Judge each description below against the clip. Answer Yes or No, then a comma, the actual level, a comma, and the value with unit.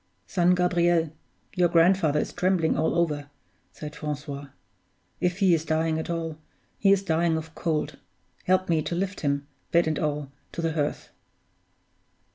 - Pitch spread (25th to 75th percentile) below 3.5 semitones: Yes, narrow, 2.5 semitones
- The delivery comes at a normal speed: Yes, average, 155 wpm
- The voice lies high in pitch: No, medium, 165 Hz